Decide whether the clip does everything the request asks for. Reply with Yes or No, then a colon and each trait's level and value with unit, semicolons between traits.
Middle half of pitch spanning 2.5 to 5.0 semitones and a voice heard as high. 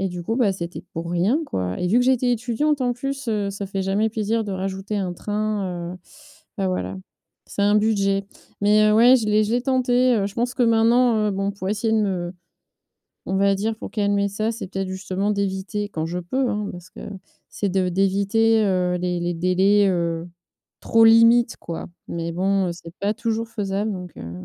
Yes: average, 3.2 semitones; high, 200 Hz